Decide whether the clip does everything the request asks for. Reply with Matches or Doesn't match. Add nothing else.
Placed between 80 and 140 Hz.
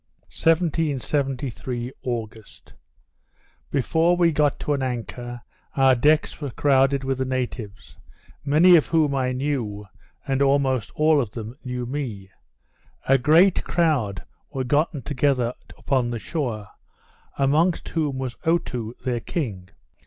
Matches